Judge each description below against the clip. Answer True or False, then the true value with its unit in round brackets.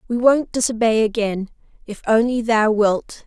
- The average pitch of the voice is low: False (225 Hz)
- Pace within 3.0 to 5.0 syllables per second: True (4.5 syllables/s)